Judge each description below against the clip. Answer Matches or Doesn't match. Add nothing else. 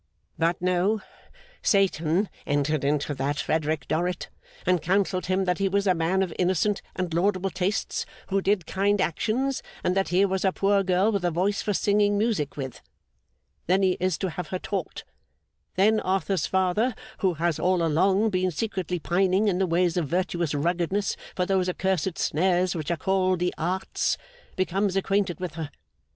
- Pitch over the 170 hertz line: Matches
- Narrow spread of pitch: Matches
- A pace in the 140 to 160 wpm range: Doesn't match